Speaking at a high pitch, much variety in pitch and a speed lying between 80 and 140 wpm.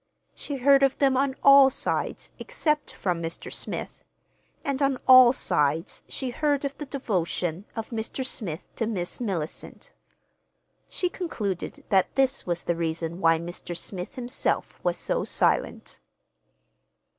Yes: high, 235 Hz; wide, 7.9 semitones; slow, 135 wpm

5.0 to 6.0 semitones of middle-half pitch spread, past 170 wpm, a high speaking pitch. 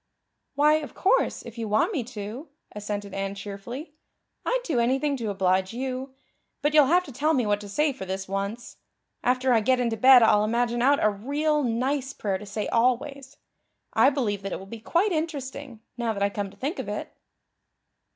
Yes: average, 5.3 semitones; average, 200 wpm; high, 245 Hz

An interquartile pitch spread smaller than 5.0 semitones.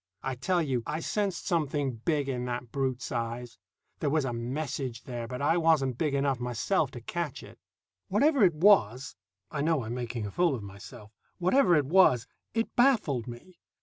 No: wide, 5.5 semitones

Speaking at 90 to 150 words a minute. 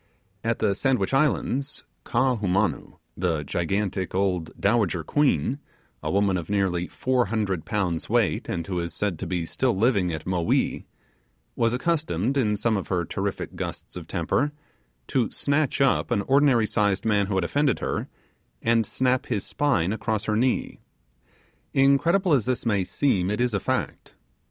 No: average, 160 wpm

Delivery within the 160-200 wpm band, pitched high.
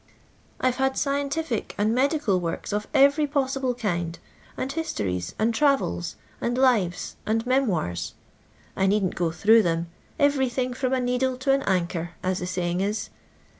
Yes: average, 165 wpm; high, 230 Hz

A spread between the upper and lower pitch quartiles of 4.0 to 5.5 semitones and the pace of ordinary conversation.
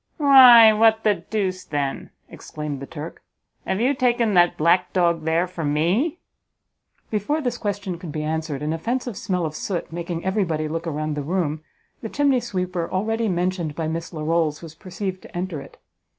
Yes: average, 5.1 semitones; average, 175 wpm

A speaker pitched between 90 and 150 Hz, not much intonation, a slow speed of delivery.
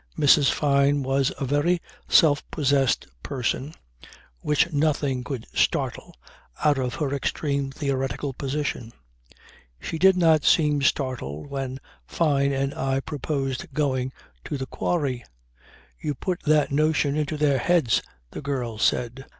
Yes: medium, 140 Hz; narrow, 2.1 semitones; slow, 130 wpm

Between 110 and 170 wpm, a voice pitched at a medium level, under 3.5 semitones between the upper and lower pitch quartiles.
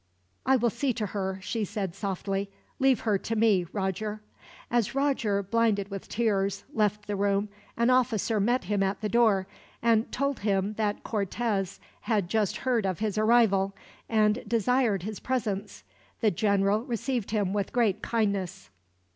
No: average, 155 wpm; high, 210 Hz; average, 2.8 semitones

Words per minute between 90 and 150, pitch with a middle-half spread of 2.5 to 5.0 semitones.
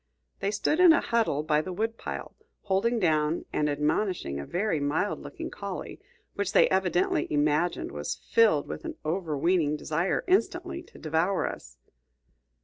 No: average, 145 wpm; wide, 5.5 semitones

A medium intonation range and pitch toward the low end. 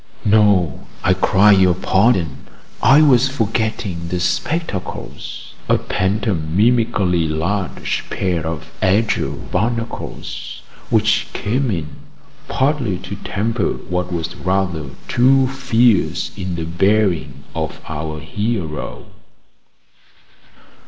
Yes: average, 5.0 semitones; very low, 95 Hz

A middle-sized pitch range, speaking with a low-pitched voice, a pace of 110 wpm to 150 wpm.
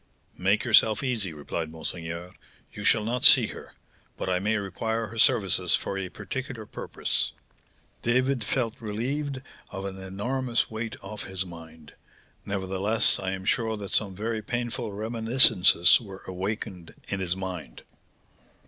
Yes: average, 3.5 semitones; low, 105 Hz; average, 140 wpm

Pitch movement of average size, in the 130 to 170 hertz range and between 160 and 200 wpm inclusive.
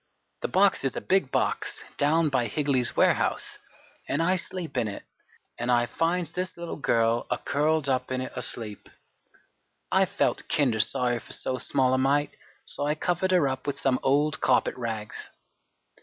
Yes: average, 4.3 semitones; low, 135 Hz; average, 170 wpm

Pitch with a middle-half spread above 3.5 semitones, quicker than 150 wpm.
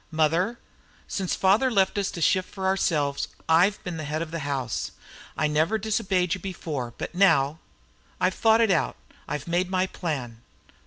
Yes: average, 4.0 semitones; average, 170 wpm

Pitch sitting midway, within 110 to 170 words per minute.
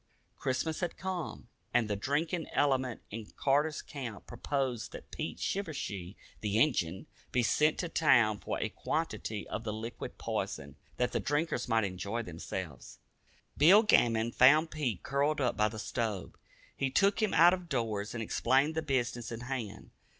No: low, 125 Hz; average, 160 wpm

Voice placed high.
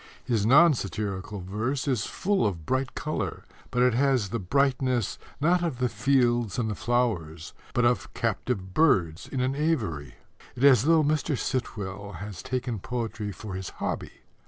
No: low, 120 Hz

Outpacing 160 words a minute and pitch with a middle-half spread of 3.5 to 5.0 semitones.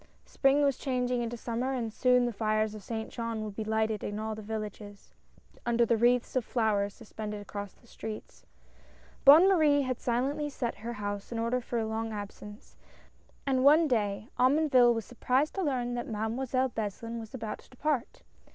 No: average, 180 wpm; average, 2.9 semitones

